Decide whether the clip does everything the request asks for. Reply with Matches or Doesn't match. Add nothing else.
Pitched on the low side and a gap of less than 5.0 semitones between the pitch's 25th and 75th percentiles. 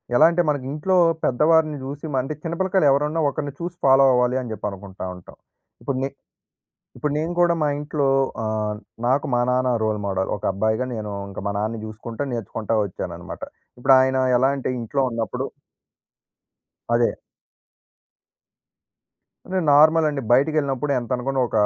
Doesn't match